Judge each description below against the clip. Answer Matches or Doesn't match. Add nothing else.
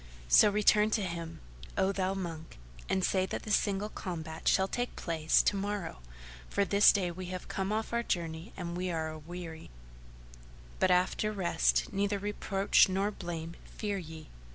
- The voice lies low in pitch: Doesn't match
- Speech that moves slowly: Doesn't match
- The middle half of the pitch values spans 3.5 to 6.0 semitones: Doesn't match